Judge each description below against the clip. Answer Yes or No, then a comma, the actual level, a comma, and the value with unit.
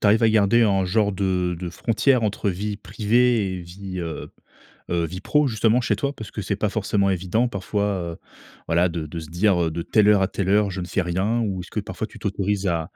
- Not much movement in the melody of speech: No, average, 3.1 semitones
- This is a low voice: Yes, low, 100 Hz